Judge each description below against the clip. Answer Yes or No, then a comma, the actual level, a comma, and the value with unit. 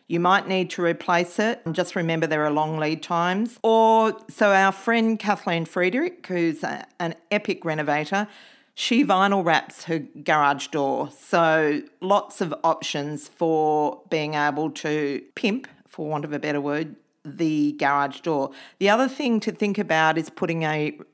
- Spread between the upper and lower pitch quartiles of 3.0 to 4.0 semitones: No, average, 4.8 semitones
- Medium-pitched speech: Yes, medium, 165 Hz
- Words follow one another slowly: No, average, 165 wpm